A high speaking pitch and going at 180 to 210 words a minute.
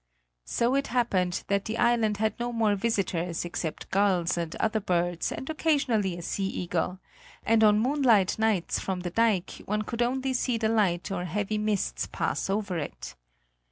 No: high, 210 Hz; average, 170 wpm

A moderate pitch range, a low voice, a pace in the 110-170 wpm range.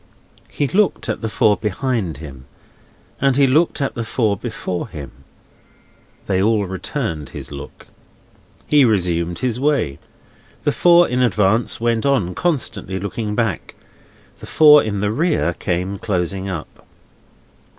No: wide, 6.1 semitones; low, 105 Hz; average, 140 wpm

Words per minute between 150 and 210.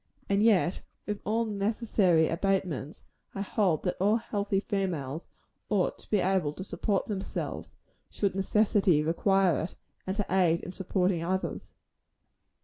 No: average, 140 wpm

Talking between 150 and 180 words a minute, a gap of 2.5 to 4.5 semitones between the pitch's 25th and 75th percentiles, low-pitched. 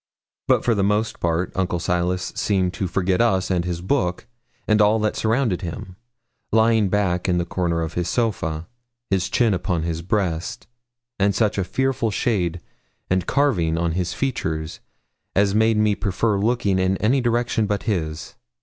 Yes: average, 170 wpm; average, 3.9 semitones; very low, 95 Hz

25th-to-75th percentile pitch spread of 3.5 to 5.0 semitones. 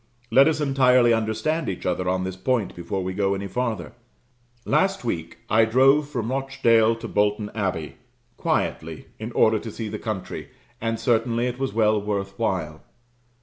Yes: average, 4.2 semitones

